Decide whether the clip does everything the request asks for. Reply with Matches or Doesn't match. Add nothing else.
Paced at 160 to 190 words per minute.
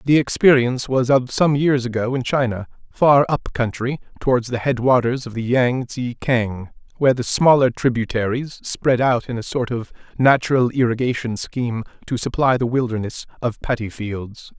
Matches